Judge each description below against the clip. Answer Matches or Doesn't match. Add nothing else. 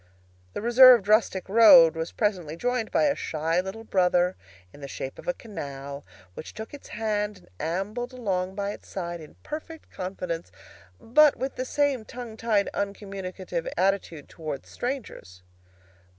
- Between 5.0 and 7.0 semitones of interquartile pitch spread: Matches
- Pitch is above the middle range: Matches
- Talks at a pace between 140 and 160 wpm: Matches